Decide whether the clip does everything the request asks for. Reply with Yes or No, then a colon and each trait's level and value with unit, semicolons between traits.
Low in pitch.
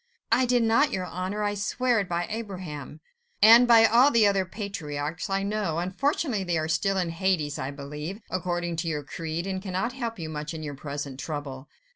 No: medium, 185 Hz